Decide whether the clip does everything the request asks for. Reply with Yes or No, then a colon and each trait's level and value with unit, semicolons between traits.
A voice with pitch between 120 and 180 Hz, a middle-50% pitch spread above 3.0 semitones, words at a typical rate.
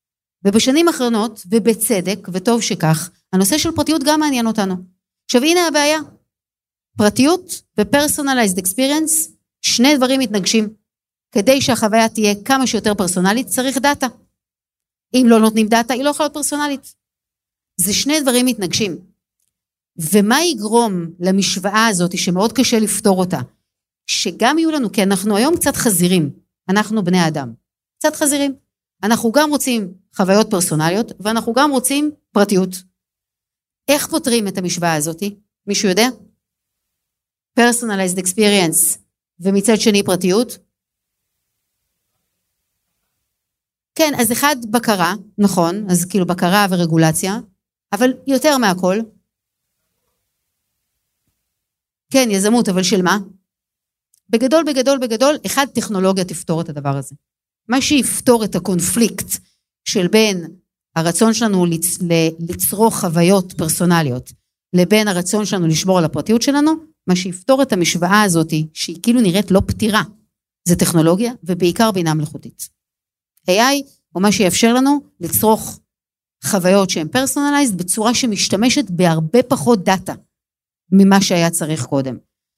No: high, 210 Hz; wide, 5.4 semitones; average, 115 wpm